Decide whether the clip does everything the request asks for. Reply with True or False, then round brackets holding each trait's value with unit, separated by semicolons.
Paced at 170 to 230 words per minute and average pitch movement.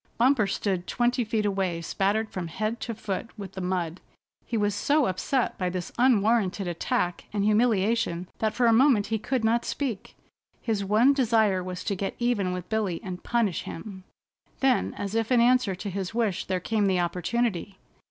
True (180 wpm; 3.9 semitones)